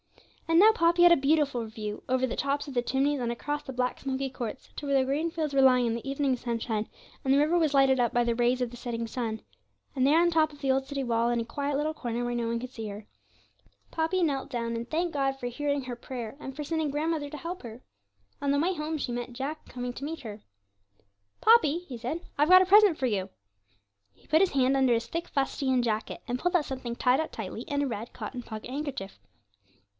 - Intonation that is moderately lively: Yes, average, 3.8 semitones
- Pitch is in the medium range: No, very high, 270 Hz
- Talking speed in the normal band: No, fast, 245 wpm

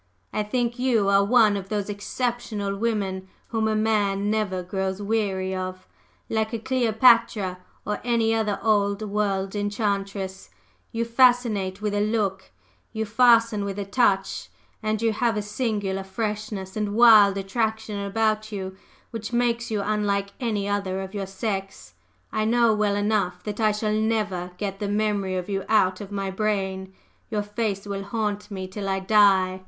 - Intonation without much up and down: Yes, narrow, 2.1 semitones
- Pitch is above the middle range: Yes, high, 205 Hz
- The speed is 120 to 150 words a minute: No, average, 160 wpm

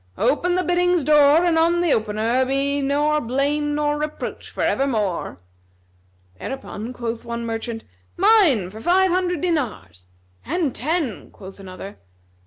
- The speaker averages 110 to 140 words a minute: Yes, slow, 135 wpm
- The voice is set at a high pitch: Yes, very high, 280 Hz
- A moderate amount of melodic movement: No, wide, 6.6 semitones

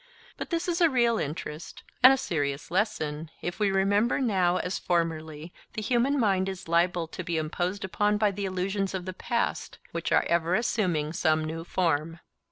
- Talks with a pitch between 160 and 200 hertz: Yes, medium, 185 Hz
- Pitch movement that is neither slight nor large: Yes, average, 4.2 semitones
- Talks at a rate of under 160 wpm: No, average, 185 wpm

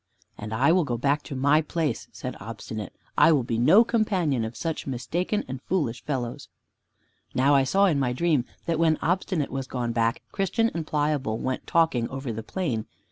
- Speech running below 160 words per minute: No, average, 190 wpm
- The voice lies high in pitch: No, medium, 140 Hz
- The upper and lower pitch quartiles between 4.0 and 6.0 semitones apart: Yes, wide, 5.5 semitones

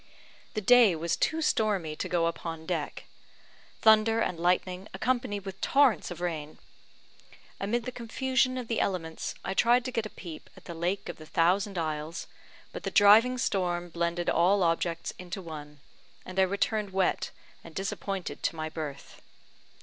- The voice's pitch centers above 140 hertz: Yes, medium, 185 Hz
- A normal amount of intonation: Yes, average, 4.6 semitones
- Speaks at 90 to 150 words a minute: No, average, 165 wpm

